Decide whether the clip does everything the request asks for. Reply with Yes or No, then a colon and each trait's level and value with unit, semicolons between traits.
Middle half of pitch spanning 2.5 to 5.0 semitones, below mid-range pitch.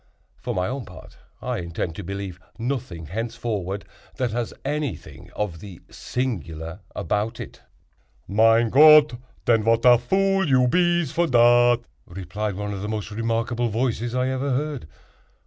Yes: average, 4.2 semitones; low, 115 Hz